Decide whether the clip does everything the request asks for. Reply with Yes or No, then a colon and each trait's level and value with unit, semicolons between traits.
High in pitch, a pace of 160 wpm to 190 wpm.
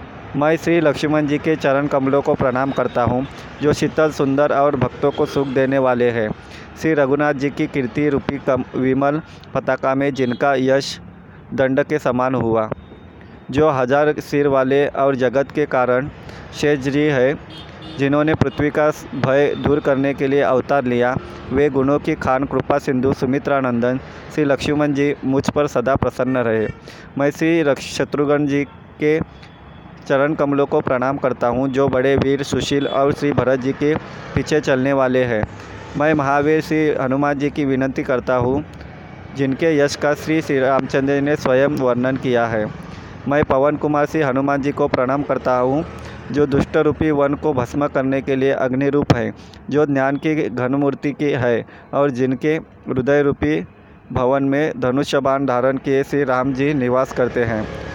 No: medium, 140 Hz; average, 165 wpm